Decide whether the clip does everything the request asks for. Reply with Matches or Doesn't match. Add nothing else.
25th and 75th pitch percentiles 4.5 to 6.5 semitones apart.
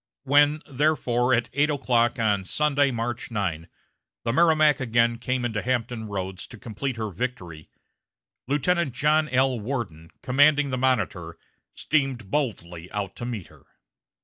Matches